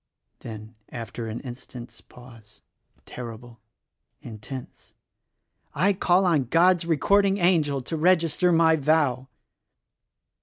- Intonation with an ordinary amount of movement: No, wide, 6.2 semitones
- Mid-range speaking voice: Yes, medium, 145 Hz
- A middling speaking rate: No, slow, 100 wpm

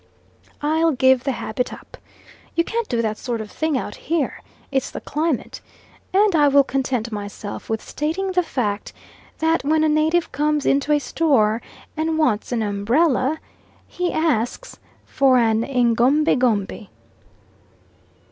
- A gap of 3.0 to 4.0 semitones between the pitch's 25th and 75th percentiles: No, average, 5.3 semitones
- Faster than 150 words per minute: No, average, 145 wpm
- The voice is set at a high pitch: Yes, very high, 275 Hz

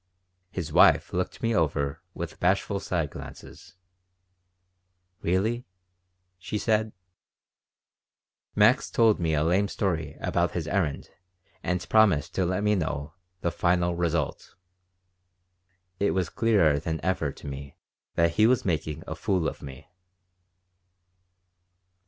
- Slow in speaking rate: Yes, slow, 120 wpm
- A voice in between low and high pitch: No, very low, 90 Hz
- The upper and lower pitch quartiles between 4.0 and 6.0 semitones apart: Yes, average, 4.3 semitones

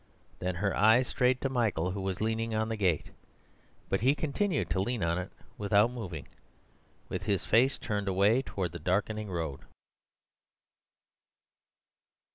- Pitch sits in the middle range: No, low, 105 Hz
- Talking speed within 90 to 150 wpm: Yes, average, 145 wpm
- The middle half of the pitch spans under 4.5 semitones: Yes, average, 4.0 semitones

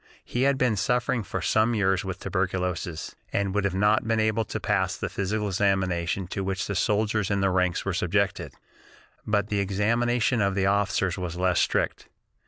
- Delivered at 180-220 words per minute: Yes, average, 185 wpm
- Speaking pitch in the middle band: No, low, 100 Hz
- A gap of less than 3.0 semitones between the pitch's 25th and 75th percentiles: Yes, narrow, 2.4 semitones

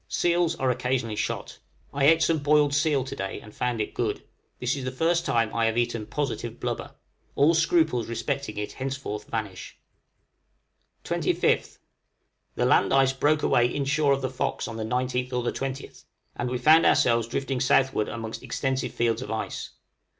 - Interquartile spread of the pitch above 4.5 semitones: No, average, 3.4 semitones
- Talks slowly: No, average, 185 wpm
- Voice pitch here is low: Yes, low, 130 Hz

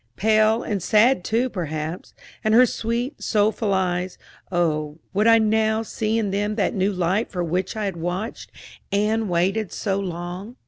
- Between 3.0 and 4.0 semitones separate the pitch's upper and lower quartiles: Yes, average, 3.6 semitones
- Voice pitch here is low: No, high, 205 Hz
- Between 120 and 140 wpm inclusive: No, average, 165 wpm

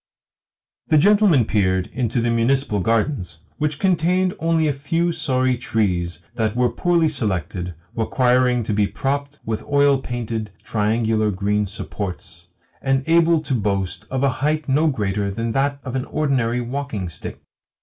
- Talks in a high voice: No, low, 125 Hz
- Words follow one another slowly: No, average, 150 wpm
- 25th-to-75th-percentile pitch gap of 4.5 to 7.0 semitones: Yes, average, 5.3 semitones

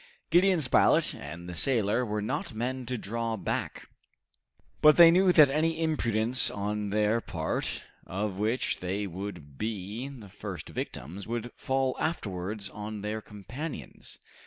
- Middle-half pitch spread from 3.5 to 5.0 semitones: Yes, average, 4.6 semitones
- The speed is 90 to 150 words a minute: Yes, average, 140 wpm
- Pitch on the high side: No, low, 110 Hz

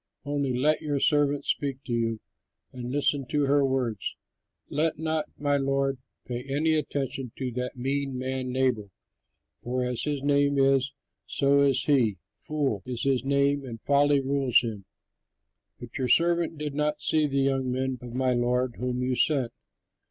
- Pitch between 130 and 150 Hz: Yes, low, 135 Hz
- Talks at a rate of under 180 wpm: Yes, average, 165 wpm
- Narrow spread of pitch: Yes, narrow, 2.2 semitones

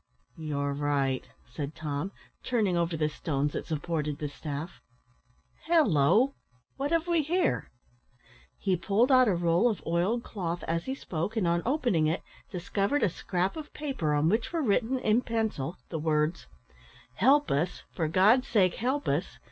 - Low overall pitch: No, medium, 180 Hz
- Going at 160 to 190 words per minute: Yes, average, 165 wpm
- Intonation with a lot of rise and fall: Yes, wide, 7.8 semitones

